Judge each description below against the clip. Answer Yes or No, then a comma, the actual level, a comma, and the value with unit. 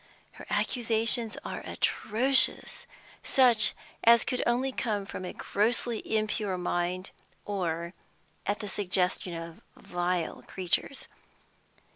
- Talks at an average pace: No, slow, 105 wpm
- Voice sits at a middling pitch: No, high, 205 Hz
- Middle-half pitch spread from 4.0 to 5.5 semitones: Yes, average, 4.4 semitones